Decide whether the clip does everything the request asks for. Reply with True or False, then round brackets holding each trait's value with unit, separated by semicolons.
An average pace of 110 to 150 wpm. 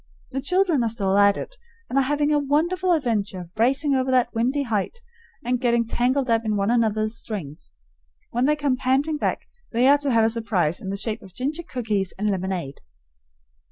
False (195 wpm)